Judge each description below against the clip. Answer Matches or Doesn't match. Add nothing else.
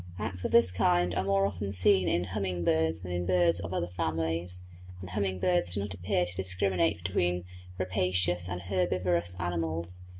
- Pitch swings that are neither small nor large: Doesn't match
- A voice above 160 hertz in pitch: Doesn't match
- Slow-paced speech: Doesn't match